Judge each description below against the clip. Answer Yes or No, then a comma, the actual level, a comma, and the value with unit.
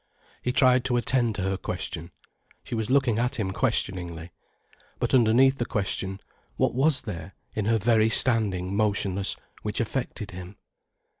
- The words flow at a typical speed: Yes, average, 150 wpm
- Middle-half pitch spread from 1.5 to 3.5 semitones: No, average, 4.4 semitones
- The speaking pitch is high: No, low, 110 Hz